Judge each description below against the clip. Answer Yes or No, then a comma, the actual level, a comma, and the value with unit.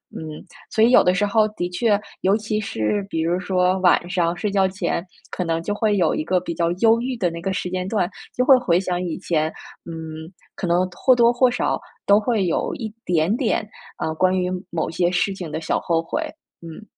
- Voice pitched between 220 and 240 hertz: No, medium, 185 Hz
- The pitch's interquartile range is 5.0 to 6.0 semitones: No, average, 3.7 semitones